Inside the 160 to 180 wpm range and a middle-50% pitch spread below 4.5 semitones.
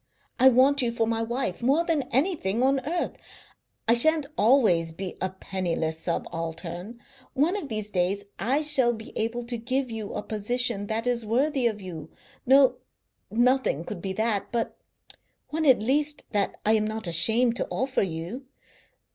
No: average, 170 wpm; average, 4.9 semitones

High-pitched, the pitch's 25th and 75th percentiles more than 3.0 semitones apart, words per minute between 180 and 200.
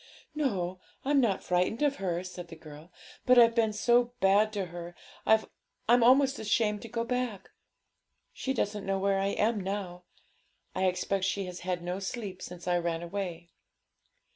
No: high, 195 Hz; average, 4.4 semitones; average, 165 wpm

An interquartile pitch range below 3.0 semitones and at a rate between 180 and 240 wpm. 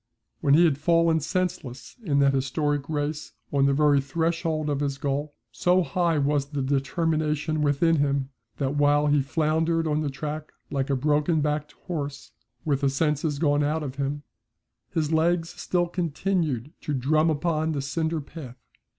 No: narrow, 2.4 semitones; average, 165 wpm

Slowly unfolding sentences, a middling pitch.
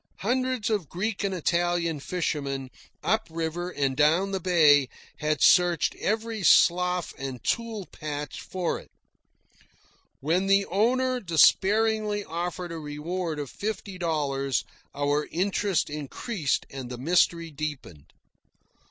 Yes: slow, 115 wpm; medium, 175 Hz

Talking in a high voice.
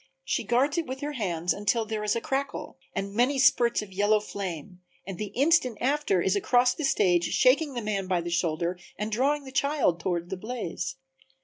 Yes: high, 215 Hz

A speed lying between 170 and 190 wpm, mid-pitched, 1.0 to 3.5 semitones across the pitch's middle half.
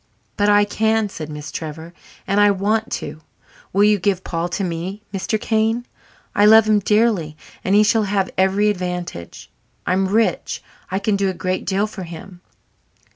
No: average, 175 wpm; high, 200 Hz; average, 2.9 semitones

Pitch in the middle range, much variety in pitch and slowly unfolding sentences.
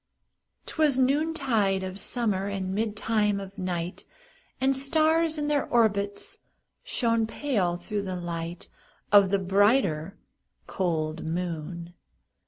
No: high, 200 Hz; wide, 6.0 semitones; slow, 110 wpm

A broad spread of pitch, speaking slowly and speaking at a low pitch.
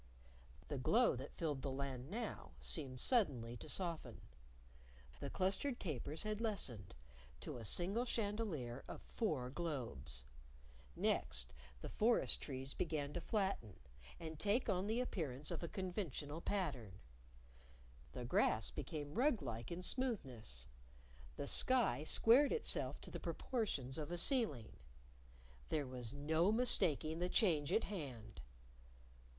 No: wide, 8.0 semitones; slow, 130 wpm; medium, 155 Hz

